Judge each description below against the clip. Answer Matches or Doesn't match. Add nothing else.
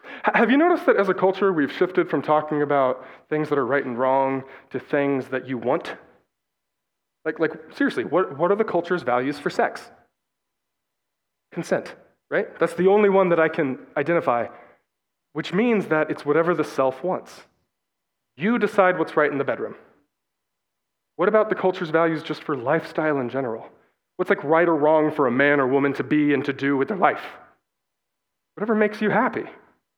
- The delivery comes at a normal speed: Matches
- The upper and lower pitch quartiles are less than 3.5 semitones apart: Doesn't match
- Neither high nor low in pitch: Matches